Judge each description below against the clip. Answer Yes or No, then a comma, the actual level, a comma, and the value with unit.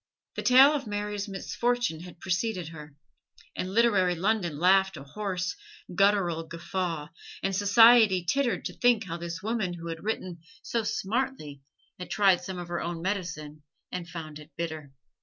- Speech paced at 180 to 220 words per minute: No, average, 160 wpm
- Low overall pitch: No, medium, 185 Hz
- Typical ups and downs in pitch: Yes, average, 3.9 semitones